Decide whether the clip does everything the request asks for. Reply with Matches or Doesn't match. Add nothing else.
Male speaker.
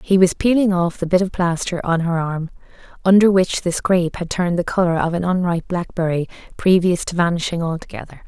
Doesn't match